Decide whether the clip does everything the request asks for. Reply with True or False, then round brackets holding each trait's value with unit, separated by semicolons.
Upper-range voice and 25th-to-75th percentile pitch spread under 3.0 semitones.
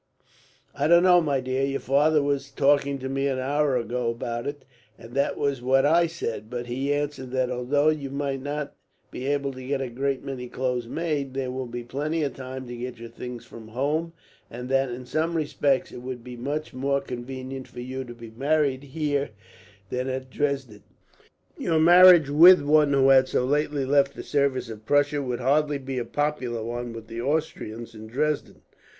False (135 Hz; 2.6 semitones)